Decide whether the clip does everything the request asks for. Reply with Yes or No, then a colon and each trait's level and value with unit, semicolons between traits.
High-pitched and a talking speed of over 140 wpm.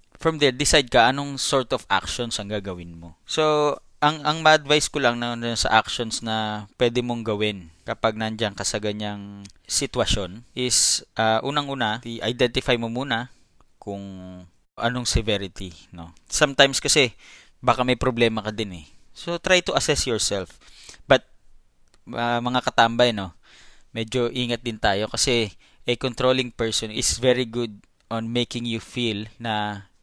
No: low, 115 Hz; average, 150 wpm